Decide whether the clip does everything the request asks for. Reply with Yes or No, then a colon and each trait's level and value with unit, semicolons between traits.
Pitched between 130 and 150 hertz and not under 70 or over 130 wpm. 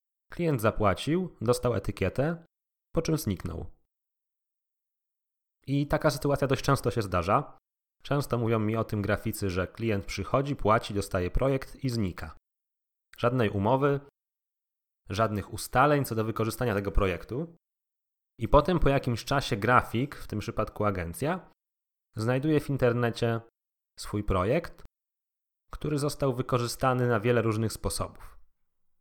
No: low, 115 Hz; average, 120 wpm